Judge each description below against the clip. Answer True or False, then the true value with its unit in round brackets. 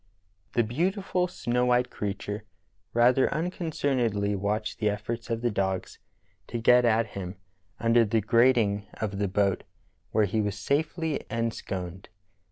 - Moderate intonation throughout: True (3.3 semitones)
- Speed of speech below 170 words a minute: True (135 wpm)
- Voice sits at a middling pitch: False (115 Hz)